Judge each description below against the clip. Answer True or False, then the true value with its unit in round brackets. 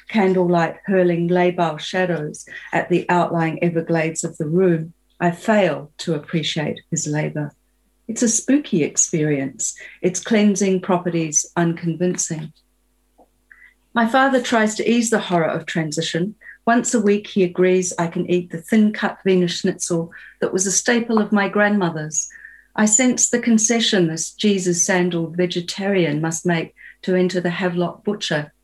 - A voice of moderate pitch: True (180 Hz)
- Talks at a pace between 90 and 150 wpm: True (140 wpm)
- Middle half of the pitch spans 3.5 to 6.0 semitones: True (3.8 semitones)